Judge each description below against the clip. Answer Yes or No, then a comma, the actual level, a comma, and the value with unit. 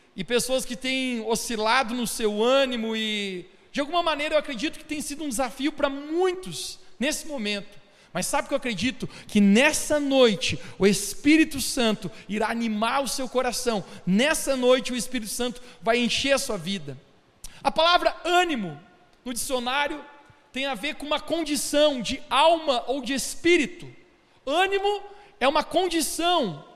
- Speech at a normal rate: Yes, average, 155 wpm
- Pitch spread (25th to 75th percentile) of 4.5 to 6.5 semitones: Yes, wide, 5.4 semitones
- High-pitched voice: Yes, very high, 260 Hz